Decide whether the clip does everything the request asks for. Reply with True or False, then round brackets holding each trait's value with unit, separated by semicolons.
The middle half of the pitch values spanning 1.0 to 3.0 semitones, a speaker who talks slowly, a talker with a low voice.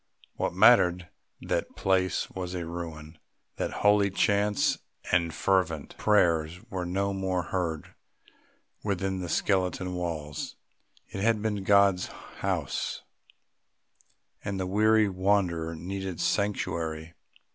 True (2.7 semitones; 115 wpm; 95 Hz)